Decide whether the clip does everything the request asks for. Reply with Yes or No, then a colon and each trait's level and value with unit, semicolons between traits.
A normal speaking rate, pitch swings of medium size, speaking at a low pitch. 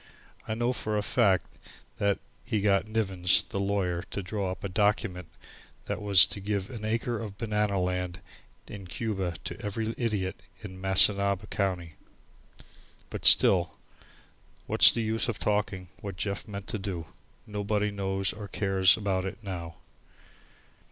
No: average, 150 wpm; narrow, 2.2 semitones; low, 100 Hz